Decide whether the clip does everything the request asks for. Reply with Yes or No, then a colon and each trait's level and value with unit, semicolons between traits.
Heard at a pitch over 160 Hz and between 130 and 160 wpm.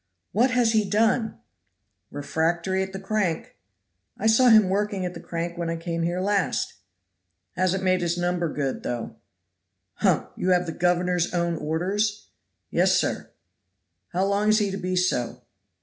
Yes: medium, 185 Hz; average, 155 wpm